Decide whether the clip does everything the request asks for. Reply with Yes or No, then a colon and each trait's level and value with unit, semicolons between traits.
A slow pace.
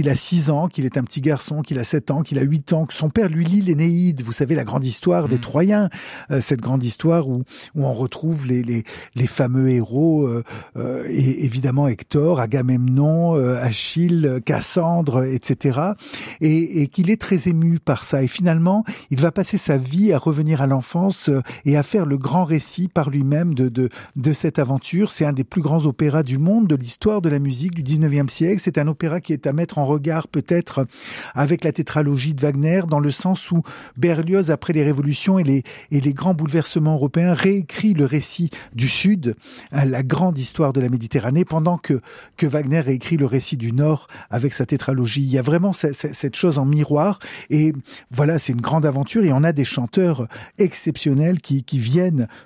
No: average, 200 wpm